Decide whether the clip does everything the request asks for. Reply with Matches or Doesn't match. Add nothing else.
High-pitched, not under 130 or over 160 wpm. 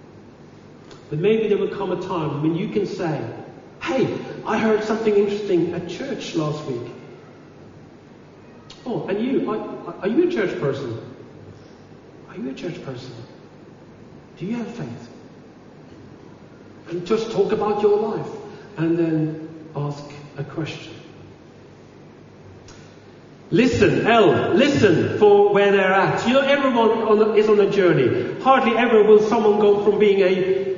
Matches